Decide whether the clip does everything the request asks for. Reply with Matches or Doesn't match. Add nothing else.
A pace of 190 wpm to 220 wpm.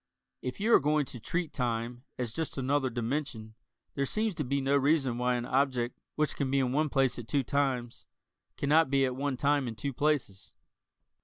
Matches